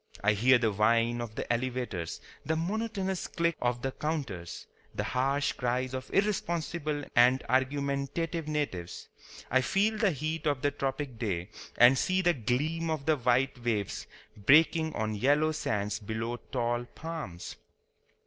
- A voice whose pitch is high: No, low, 130 Hz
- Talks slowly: No, average, 145 wpm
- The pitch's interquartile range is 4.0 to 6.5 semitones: Yes, average, 4.9 semitones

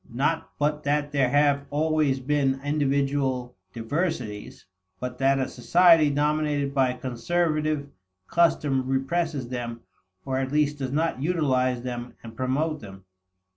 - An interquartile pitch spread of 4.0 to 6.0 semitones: No, average, 2.9 semitones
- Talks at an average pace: No, slow, 130 wpm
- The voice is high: No, medium, 140 Hz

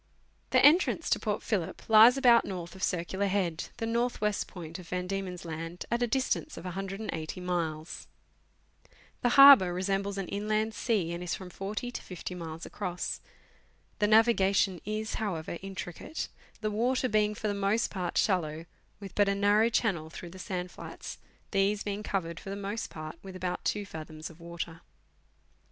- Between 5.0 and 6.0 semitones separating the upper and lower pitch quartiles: No, average, 3.5 semitones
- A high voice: Yes, high, 195 Hz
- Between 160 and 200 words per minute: Yes, average, 175 wpm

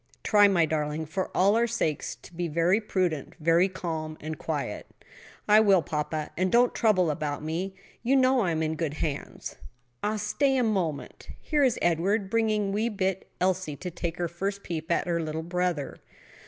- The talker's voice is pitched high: No, medium, 180 Hz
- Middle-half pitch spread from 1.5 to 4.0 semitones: No, average, 4.6 semitones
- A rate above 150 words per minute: Yes, average, 180 wpm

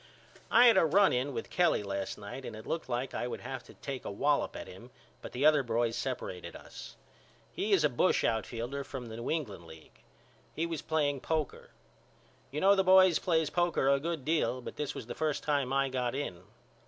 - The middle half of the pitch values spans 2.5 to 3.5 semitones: No, average, 4.9 semitones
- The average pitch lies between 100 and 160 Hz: Yes, medium, 140 Hz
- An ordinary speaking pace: No, fast, 215 wpm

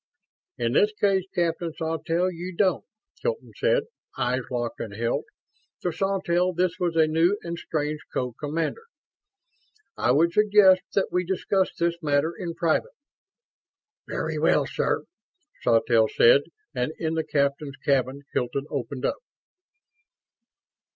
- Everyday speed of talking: No, slow, 130 wpm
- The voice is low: No, medium, 165 Hz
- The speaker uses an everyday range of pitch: Yes, average, 4.6 semitones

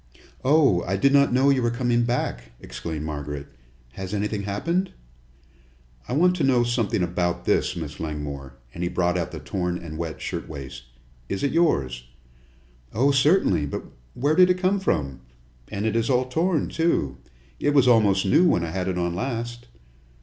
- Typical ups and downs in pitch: No, wide, 8.7 semitones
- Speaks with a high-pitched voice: No, low, 100 Hz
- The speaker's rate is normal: Yes, average, 175 wpm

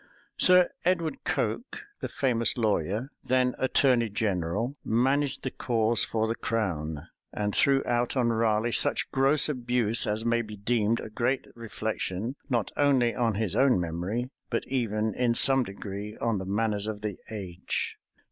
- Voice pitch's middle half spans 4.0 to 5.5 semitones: No, average, 3.2 semitones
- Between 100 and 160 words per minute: Yes, average, 155 wpm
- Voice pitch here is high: No, low, 115 Hz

